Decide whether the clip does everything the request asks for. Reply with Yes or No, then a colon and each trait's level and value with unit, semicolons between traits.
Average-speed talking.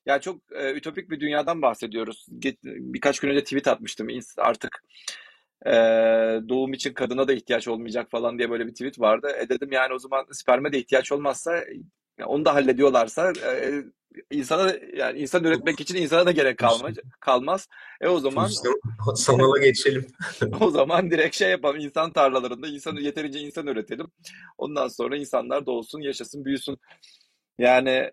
No: fast, 160 wpm